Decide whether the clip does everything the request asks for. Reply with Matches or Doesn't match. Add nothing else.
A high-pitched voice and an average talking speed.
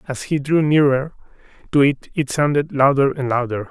Doesn't match